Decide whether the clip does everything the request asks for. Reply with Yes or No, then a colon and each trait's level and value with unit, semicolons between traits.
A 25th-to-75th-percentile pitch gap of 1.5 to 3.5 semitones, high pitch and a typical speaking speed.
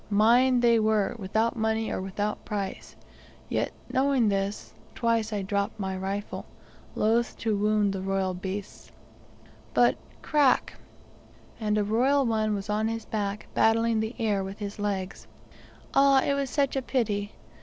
Yes: narrow, 2.5 semitones; high, 215 Hz; average, 150 wpm